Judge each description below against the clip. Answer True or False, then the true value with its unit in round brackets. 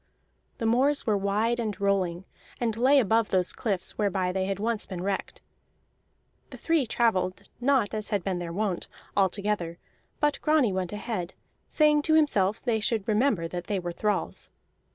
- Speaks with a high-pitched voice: True (210 Hz)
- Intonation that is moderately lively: True (4.0 semitones)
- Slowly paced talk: False (170 wpm)